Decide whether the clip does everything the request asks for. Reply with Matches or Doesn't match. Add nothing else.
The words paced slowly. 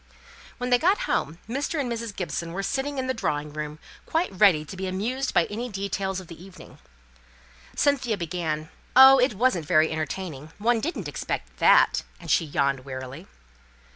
Doesn't match